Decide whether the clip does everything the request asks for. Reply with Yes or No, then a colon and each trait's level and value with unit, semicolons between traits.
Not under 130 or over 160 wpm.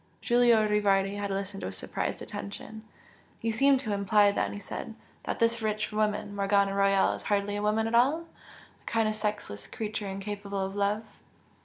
No: average, 175 wpm